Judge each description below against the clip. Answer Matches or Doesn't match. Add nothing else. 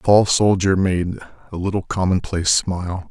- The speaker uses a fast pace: Doesn't match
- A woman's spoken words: Doesn't match